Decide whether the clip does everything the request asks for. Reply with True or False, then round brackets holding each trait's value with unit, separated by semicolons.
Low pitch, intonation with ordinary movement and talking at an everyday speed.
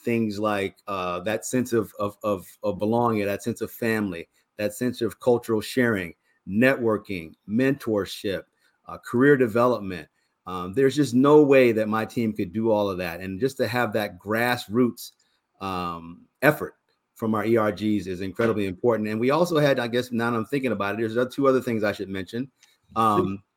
True (110 Hz; 3.5 semitones; 180 wpm)